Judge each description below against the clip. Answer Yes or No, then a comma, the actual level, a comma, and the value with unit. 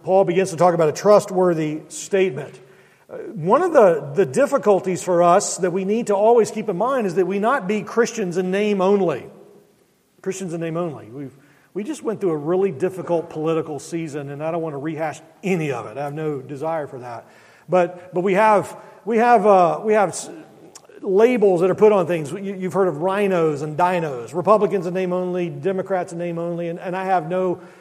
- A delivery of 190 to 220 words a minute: Yes, fast, 205 wpm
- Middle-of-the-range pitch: Yes, medium, 180 Hz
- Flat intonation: No, average, 3.3 semitones